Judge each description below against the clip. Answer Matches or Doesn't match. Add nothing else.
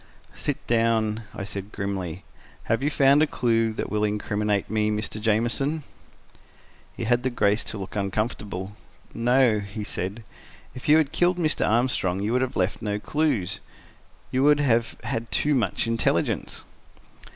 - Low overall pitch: Matches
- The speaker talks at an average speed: Matches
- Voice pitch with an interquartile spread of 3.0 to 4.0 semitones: Matches